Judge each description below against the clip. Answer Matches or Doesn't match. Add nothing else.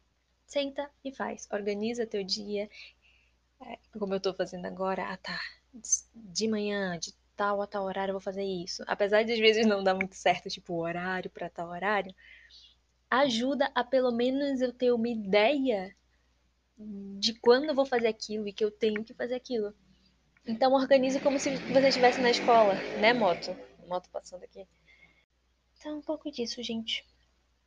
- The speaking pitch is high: Matches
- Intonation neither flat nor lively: Matches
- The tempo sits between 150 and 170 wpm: Matches